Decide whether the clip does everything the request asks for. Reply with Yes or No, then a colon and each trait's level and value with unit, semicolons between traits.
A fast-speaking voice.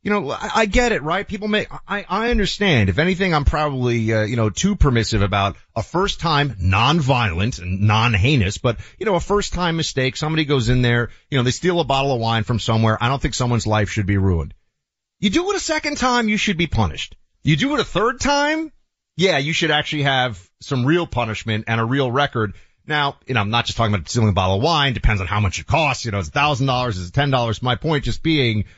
Yes: fast, 245 wpm